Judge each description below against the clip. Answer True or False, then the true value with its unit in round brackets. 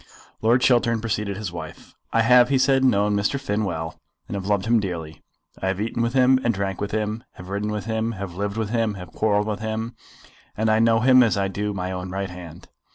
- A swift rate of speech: True (235 wpm)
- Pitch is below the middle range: True (105 Hz)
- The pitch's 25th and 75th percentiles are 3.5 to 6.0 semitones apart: False (2.9 semitones)